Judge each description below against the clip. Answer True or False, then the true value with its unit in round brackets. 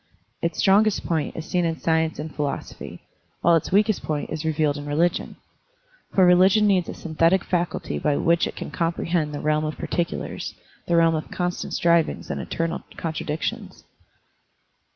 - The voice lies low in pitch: False (165 Hz)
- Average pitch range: False (2.2 semitones)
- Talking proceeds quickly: False (170 wpm)